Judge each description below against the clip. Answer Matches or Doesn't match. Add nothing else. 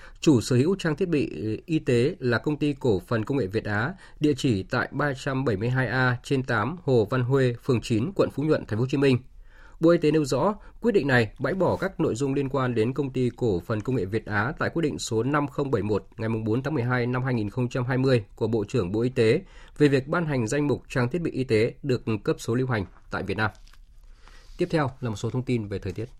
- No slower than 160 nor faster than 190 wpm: Doesn't match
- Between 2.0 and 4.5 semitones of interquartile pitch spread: Matches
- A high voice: Doesn't match